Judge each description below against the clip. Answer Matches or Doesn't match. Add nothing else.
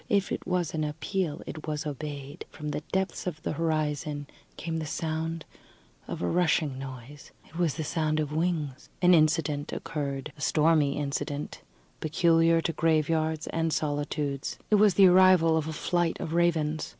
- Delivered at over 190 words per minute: Doesn't match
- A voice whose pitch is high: Doesn't match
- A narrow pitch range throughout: Matches